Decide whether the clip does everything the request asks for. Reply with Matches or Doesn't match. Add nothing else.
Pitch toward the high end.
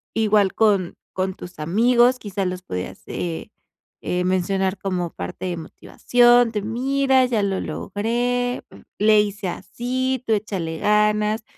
Matches